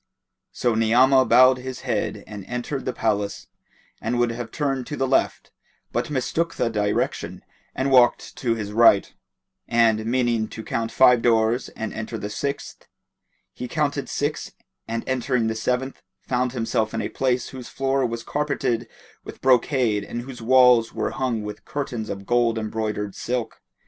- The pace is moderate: Yes, average, 160 wpm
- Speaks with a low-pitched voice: Yes, low, 120 Hz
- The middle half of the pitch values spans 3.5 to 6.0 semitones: No, average, 2.7 semitones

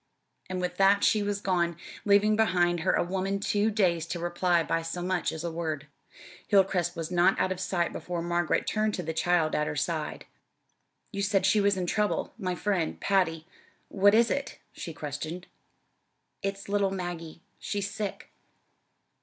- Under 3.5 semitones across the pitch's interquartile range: Yes, average, 2.7 semitones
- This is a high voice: No, medium, 180 Hz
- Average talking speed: Yes, average, 170 wpm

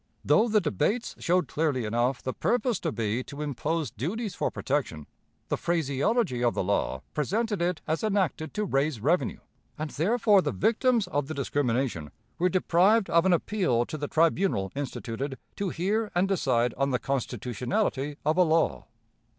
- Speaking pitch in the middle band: Yes, medium, 155 Hz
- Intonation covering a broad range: Yes, wide, 6.9 semitones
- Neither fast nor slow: Yes, average, 165 wpm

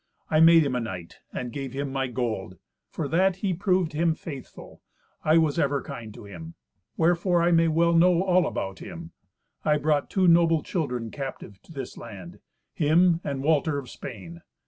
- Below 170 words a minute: No, average, 175 wpm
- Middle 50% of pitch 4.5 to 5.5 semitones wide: Yes, average, 5.2 semitones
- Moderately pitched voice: Yes, medium, 150 Hz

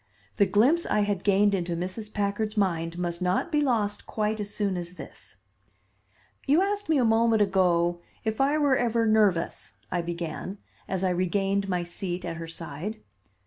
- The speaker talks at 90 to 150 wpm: No, average, 175 wpm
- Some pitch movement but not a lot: Yes, average, 3.9 semitones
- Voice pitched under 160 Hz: No, high, 200 Hz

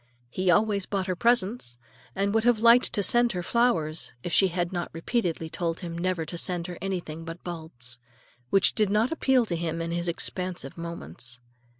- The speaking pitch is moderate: Yes, medium, 175 Hz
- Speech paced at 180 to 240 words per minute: Yes, average, 185 wpm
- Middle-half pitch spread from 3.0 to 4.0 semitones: Yes, average, 3.6 semitones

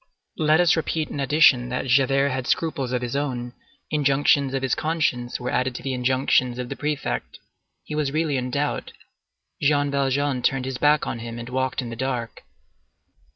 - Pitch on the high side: No, low, 135 Hz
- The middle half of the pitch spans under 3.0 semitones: Yes, narrow, 2.6 semitones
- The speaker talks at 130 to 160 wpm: No, average, 185 wpm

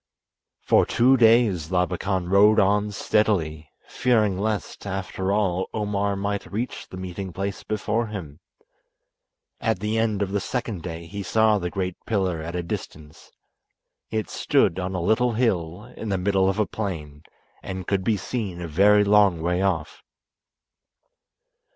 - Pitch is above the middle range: No, low, 100 Hz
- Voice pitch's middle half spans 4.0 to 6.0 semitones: No, average, 2.9 semitones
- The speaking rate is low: No, average, 150 wpm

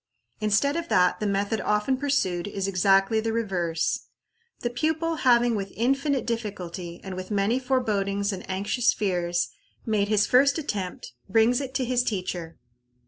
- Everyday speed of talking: Yes, average, 150 wpm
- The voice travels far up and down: No, average, 4.4 semitones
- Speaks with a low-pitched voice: No, high, 210 Hz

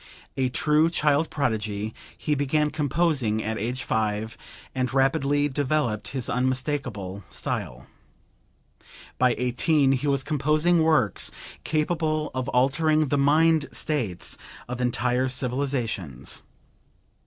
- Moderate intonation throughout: Yes, average, 3.8 semitones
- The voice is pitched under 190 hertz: Yes, low, 135 Hz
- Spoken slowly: Yes, slow, 110 wpm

